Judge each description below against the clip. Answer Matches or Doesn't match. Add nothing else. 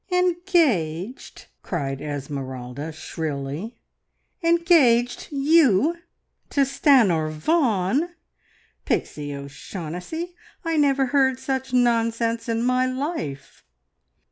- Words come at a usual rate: Doesn't match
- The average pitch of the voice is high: Matches